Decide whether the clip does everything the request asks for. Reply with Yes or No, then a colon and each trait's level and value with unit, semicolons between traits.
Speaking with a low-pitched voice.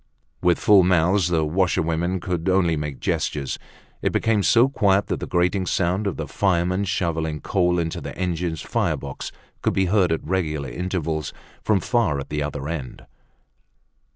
Yes: very low, 90 Hz